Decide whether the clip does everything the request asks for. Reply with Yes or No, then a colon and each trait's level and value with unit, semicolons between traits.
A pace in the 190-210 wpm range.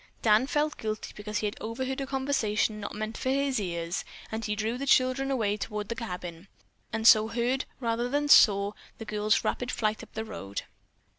Yes: average, 195 wpm